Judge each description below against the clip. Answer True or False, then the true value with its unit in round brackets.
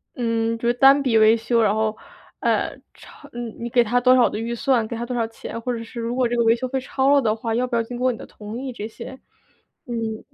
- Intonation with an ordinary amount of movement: False (1.7 semitones)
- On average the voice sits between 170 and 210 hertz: False (235 Hz)